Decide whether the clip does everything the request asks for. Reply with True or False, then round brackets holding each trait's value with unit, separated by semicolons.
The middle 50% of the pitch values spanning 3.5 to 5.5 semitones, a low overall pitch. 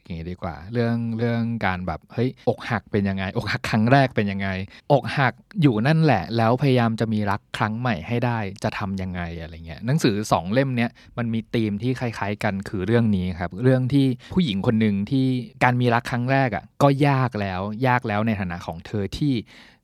True (4.2 semitones; 115 Hz)